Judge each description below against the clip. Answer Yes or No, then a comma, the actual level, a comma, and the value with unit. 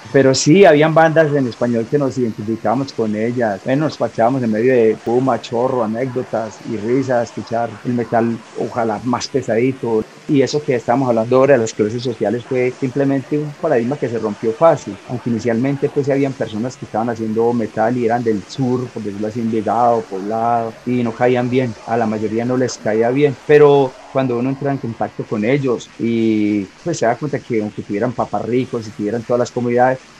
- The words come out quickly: Yes, fast, 195 wpm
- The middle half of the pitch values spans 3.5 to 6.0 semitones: No, average, 2.8 semitones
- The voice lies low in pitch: Yes, low, 120 Hz